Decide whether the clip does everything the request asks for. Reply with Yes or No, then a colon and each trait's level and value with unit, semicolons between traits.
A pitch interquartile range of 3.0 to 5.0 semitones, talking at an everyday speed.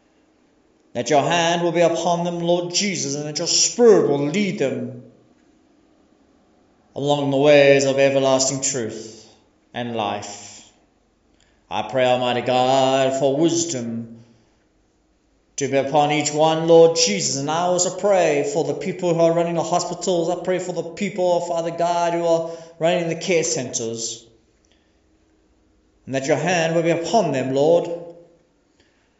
No: wide, 5.5 semitones; average, 150 wpm